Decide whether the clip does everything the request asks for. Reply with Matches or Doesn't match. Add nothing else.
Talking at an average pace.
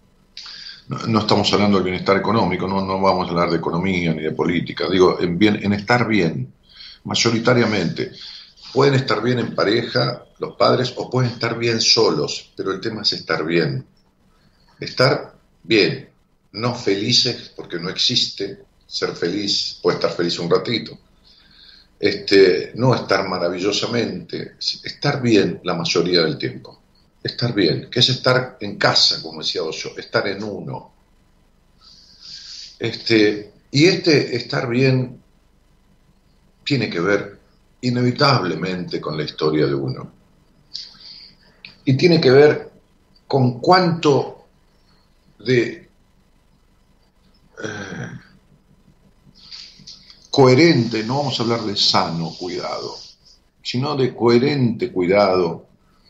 Doesn't match